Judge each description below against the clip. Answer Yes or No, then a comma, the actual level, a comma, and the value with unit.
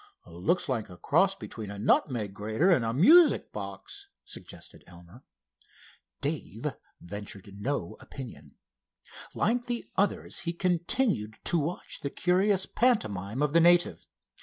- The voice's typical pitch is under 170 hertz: Yes, medium, 140 Hz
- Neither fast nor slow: No, slow, 130 wpm